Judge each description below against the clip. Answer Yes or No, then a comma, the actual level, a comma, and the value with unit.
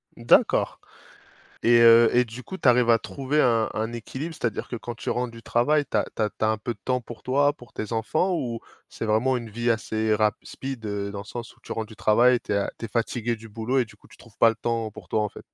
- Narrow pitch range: Yes, narrow, 2.2 semitones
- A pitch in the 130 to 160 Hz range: No, low, 115 Hz